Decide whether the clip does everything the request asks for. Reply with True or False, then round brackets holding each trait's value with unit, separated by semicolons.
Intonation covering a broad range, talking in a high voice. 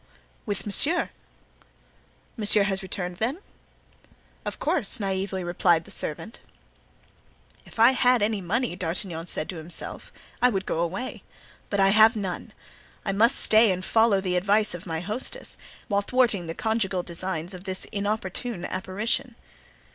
False (3.6 semitones; 195 Hz)